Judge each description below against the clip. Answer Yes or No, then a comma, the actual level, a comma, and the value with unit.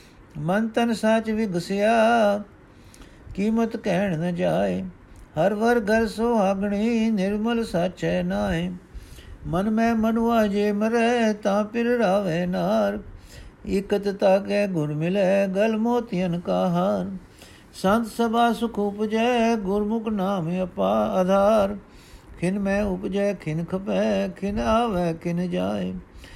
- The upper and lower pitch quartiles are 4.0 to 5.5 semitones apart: No, average, 3.3 semitones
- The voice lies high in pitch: Yes, high, 200 Hz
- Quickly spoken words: No, average, 115 wpm